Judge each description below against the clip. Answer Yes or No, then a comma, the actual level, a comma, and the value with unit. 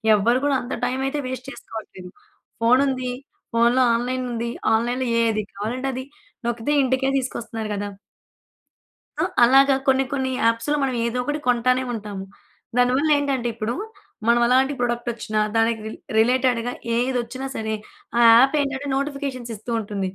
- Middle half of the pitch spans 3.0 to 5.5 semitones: No, narrow, 2.4 semitones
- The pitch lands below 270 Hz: Yes, high, 245 Hz